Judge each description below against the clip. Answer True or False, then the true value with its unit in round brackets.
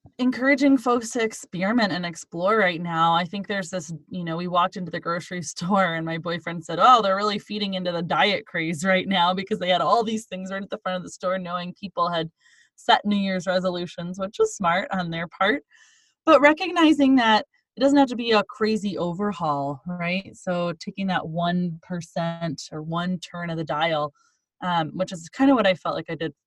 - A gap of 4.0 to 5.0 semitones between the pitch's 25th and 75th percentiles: False (3.4 semitones)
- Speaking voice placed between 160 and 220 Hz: True (185 Hz)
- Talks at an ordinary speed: False (210 wpm)